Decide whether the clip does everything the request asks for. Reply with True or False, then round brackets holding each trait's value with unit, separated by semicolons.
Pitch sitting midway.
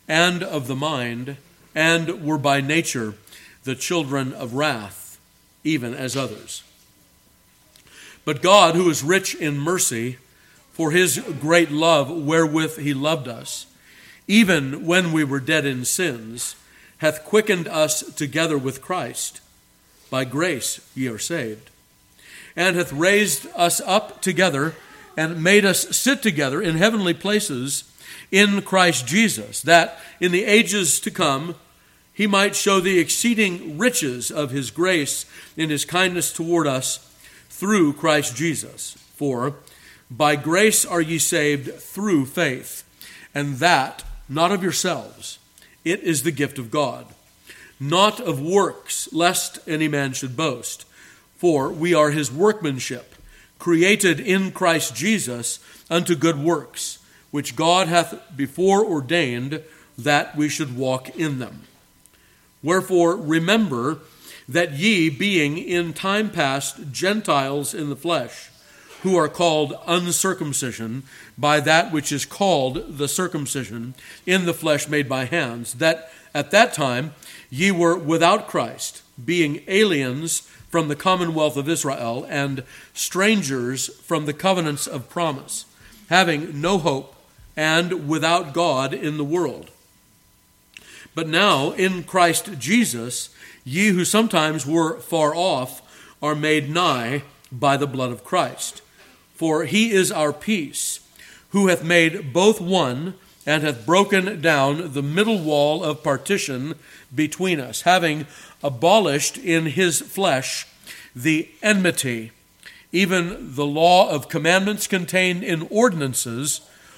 True (160 Hz)